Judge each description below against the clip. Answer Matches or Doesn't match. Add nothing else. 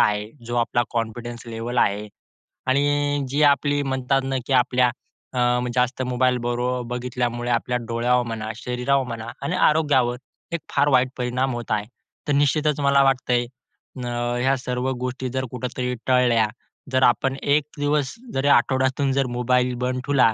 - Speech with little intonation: Matches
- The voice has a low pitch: Matches